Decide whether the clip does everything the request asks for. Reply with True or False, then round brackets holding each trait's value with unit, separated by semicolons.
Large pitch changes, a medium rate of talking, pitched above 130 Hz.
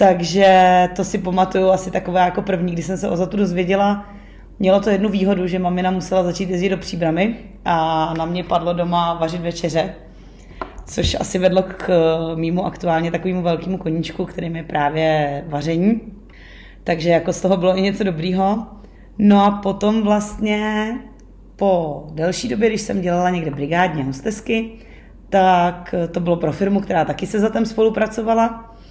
False (2.9 semitones; 160 wpm; 185 Hz)